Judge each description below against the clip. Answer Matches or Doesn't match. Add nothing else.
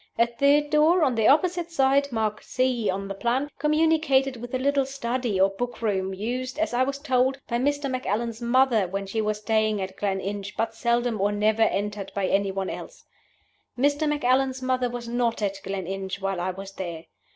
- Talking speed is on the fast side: Doesn't match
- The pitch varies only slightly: Doesn't match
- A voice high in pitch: Matches